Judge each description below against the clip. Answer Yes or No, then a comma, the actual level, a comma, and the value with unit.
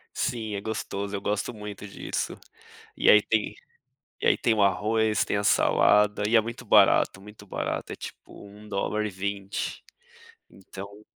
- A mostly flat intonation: Yes, narrow, 1.2 semitones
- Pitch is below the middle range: Yes, low, 105 Hz